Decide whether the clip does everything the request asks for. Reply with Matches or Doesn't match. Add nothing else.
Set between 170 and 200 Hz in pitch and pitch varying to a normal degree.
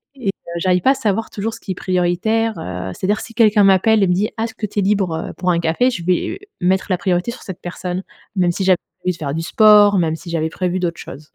Matches